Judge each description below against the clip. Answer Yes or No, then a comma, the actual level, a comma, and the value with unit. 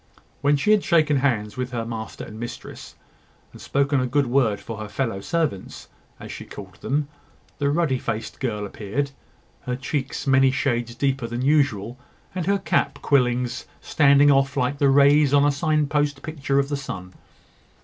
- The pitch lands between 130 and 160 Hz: Yes, low, 135 Hz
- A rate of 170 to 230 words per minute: Yes, average, 175 wpm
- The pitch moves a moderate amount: Yes, average, 3.4 semitones